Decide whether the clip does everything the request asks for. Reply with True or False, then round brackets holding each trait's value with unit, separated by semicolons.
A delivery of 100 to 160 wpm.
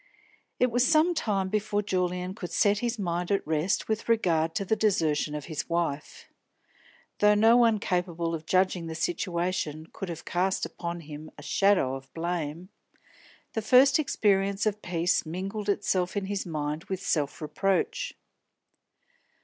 True (155 wpm)